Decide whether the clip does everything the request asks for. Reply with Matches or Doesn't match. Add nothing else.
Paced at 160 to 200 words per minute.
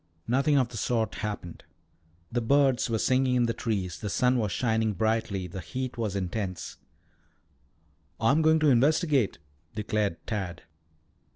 Doesn't match